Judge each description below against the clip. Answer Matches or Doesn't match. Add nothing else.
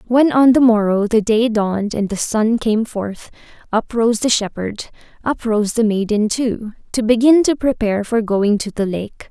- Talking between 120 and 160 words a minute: Doesn't match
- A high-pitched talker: Matches